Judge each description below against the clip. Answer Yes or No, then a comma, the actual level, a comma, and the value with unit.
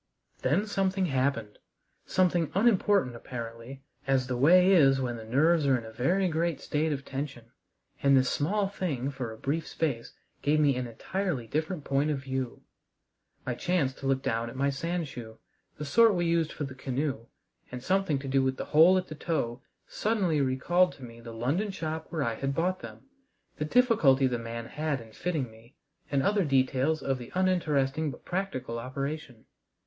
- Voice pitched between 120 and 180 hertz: Yes, medium, 140 Hz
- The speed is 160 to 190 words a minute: Yes, average, 185 wpm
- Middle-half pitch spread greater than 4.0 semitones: Yes, average, 4.9 semitones